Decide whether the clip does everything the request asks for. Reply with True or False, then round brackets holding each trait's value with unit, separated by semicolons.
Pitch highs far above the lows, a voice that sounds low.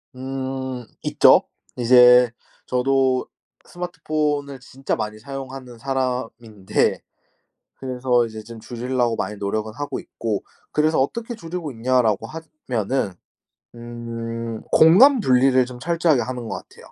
False (2.8 semitones; 125 Hz)